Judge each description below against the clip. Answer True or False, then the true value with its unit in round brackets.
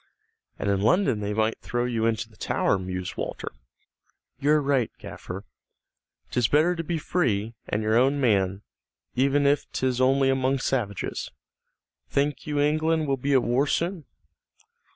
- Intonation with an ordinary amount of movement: True (4.6 semitones)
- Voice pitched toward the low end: True (130 Hz)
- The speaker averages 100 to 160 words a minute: True (150 wpm)